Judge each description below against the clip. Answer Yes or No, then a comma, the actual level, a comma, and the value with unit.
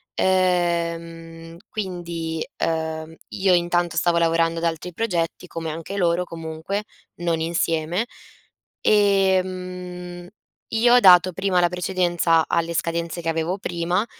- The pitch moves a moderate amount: No, narrow, 1.7 semitones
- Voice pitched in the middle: Yes, medium, 170 Hz